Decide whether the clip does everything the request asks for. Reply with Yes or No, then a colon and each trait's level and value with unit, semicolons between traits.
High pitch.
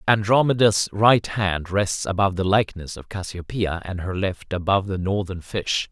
No: very low, 95 Hz